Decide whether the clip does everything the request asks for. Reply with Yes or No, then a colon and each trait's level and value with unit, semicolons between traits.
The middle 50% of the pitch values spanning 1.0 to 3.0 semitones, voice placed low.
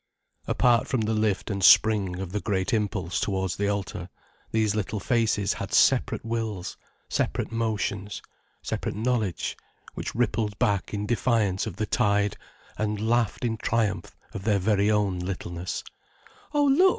Yes: narrow, 2.4 semitones; low, 105 Hz